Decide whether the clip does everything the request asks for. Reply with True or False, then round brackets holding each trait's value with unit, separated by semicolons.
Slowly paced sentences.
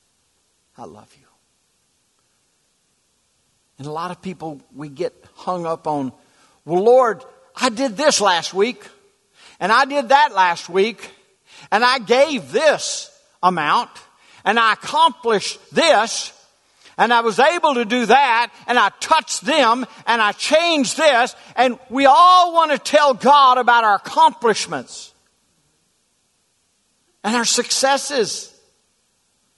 True (130 wpm)